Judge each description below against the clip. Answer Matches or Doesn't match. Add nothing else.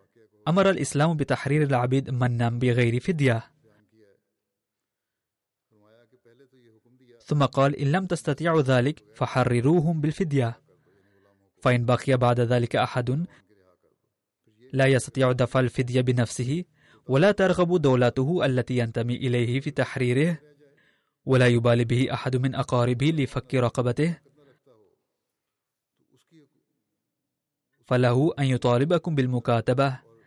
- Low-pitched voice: Matches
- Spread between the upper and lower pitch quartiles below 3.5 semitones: Matches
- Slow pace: Doesn't match